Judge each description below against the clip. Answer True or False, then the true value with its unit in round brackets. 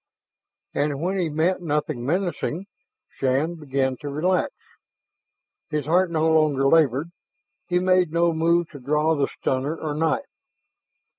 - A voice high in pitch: False (160 Hz)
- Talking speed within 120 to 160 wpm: True (135 wpm)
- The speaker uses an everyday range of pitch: True (3.1 semitones)